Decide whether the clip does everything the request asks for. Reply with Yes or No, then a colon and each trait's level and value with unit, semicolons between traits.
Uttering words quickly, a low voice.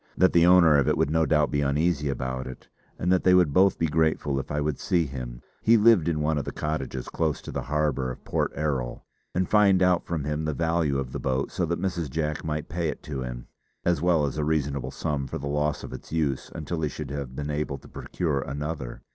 Yes: fast, 245 wpm; very low, 75 Hz